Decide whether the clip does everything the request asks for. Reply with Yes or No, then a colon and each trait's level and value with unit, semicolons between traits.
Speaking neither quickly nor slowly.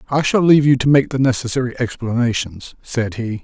Yes: average, 190 wpm